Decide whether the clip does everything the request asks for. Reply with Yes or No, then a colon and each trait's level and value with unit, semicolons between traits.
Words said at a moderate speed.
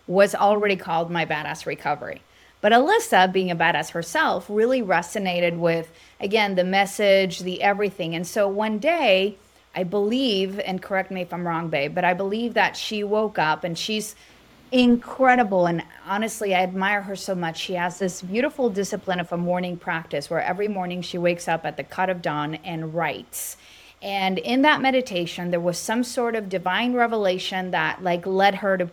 Yes: average, 185 wpm